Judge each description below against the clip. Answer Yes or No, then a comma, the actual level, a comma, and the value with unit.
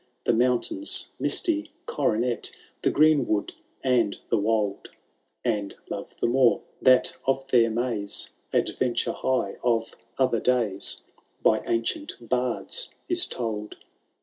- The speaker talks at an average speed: No, slow, 115 wpm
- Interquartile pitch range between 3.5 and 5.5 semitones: No, average, 3.0 semitones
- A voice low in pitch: Yes, low, 120 Hz